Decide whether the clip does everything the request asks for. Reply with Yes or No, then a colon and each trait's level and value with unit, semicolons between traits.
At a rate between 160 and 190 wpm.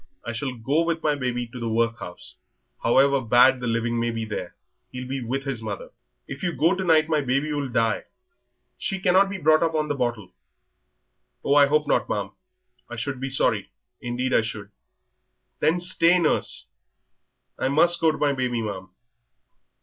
Yes: average, 180 wpm